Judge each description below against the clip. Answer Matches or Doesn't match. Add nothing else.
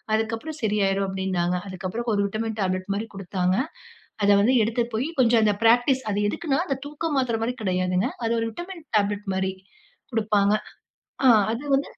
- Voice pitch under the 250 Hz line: Matches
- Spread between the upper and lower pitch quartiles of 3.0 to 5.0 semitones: Matches